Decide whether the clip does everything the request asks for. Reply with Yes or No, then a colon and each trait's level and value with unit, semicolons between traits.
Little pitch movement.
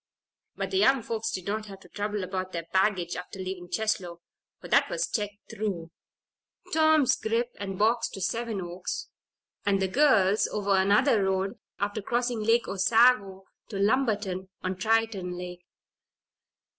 No: average, 3.2 semitones